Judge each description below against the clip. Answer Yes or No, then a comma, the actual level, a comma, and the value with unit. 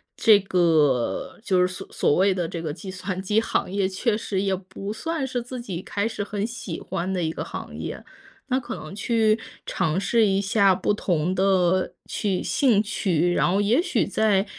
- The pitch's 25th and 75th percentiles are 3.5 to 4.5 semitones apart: No, average, 3.0 semitones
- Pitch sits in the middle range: No, high, 195 Hz